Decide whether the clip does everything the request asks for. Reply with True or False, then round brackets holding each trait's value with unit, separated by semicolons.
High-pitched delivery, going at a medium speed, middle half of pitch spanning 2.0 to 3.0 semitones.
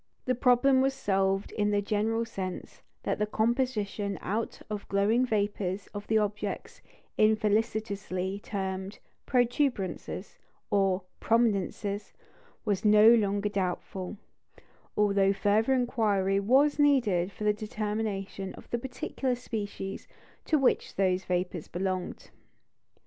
False (210 Hz; 115 wpm; 2.6 semitones)